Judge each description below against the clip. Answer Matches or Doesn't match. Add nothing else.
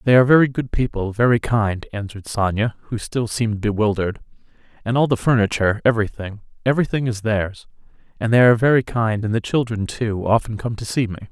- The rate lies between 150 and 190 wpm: Matches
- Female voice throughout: Doesn't match